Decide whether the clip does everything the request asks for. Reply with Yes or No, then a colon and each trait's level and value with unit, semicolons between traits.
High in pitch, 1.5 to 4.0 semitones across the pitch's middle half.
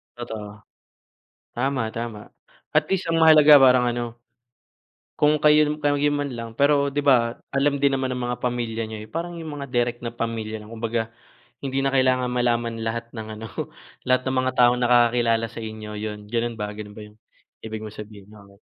No: low, 120 Hz; average, 3.4 semitones